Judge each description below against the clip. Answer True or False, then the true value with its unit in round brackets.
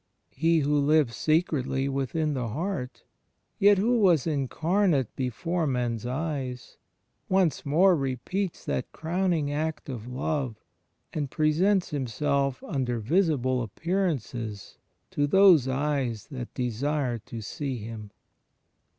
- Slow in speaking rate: True (115 wpm)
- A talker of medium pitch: True (145 Hz)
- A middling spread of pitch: True (4.6 semitones)